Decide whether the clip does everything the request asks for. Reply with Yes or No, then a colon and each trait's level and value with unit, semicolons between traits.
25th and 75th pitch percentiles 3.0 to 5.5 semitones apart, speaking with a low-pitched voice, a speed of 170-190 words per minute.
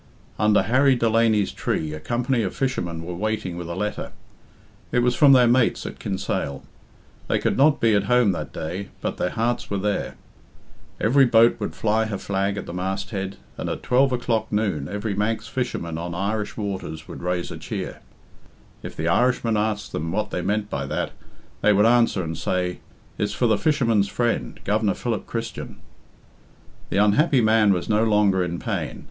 Yes: average, 3.6 semitones; low, 105 Hz; average, 180 wpm